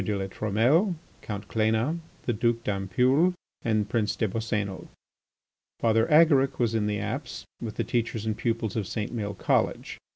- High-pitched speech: No, low, 110 Hz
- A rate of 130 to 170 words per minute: Yes, average, 160 wpm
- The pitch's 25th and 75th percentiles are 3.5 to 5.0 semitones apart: No, narrow, 2.5 semitones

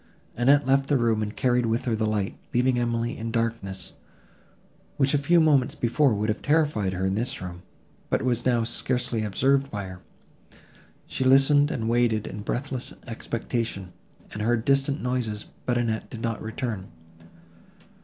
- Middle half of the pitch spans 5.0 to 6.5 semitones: No, average, 3.3 semitones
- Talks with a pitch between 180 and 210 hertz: No, low, 120 Hz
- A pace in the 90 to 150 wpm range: No, average, 165 wpm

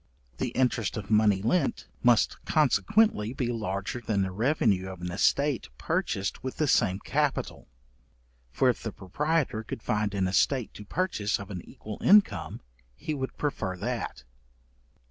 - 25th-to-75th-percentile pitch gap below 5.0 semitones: No, average, 5.3 semitones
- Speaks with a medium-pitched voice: No, low, 110 Hz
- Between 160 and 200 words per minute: No, average, 150 wpm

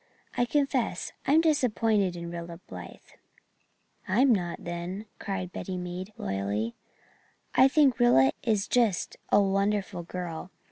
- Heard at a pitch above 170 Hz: Yes, high, 190 Hz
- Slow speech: Yes, slow, 130 wpm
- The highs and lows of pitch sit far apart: Yes, wide, 5.7 semitones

